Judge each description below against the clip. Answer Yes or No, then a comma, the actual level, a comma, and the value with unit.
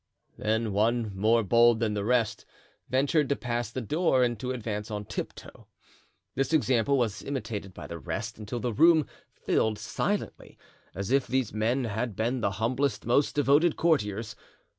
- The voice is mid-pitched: No, low, 120 Hz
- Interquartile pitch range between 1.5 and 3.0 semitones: No, average, 3.7 semitones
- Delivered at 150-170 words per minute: Yes, average, 160 wpm